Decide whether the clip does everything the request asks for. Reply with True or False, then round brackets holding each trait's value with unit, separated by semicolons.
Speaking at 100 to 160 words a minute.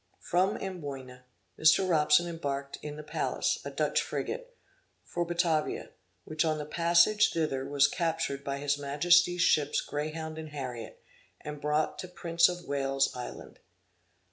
True (140 wpm)